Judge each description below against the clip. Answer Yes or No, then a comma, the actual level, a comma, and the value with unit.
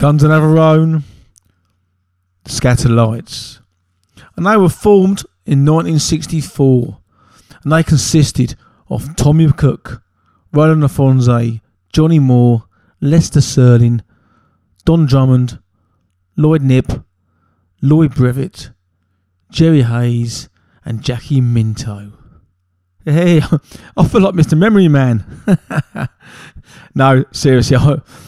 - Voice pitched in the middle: No, low, 125 Hz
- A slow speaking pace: Yes, slow, 95 wpm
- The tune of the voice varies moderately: No, wide, 6.8 semitones